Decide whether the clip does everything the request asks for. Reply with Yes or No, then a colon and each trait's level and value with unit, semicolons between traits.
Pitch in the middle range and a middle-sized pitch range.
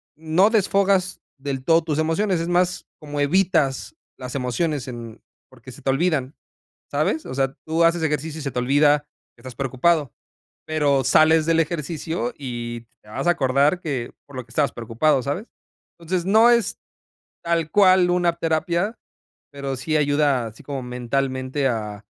Yes: medium, 150 Hz; average, 4.4 semitones